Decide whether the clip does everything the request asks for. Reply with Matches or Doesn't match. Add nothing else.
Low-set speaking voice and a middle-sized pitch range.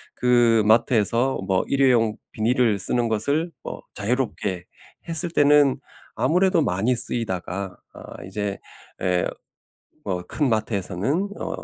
Matches